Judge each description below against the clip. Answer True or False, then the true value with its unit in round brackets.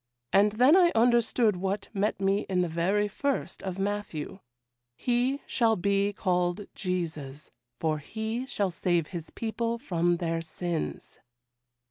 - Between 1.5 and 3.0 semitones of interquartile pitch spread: False (4.4 semitones)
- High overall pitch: True (195 Hz)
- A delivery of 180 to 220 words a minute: False (135 wpm)